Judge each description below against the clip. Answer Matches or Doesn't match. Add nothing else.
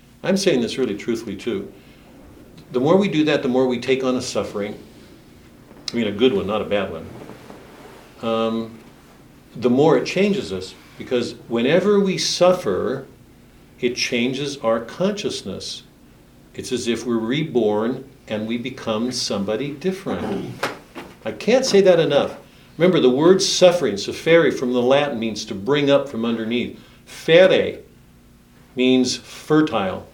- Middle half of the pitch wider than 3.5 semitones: Matches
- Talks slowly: Doesn't match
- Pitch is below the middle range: Matches